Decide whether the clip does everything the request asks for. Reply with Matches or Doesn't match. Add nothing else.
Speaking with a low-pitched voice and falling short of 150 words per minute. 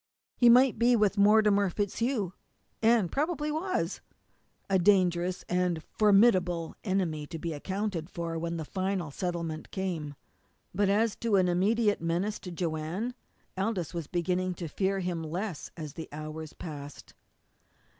Doesn't match